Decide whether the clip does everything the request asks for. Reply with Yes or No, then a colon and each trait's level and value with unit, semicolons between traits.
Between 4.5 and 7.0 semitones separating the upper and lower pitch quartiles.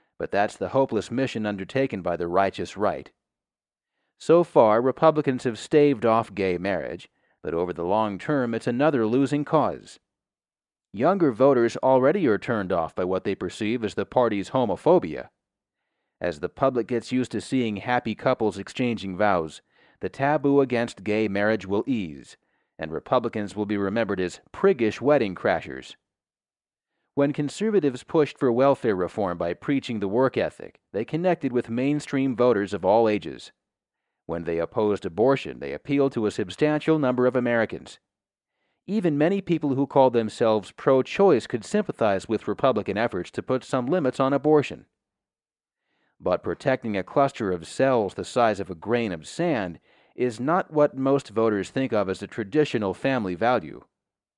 Yes: average, 5.0 semitones